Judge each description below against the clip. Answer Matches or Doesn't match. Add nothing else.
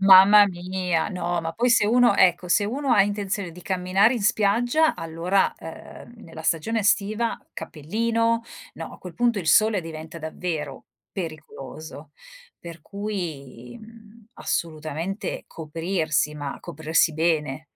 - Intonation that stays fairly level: Doesn't match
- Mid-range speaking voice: Matches